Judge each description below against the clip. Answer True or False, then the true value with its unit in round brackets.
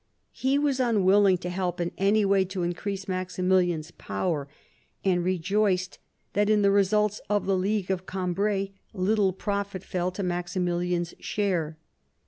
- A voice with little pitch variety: True (2.2 semitones)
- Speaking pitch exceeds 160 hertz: True (190 Hz)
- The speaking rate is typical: True (145 wpm)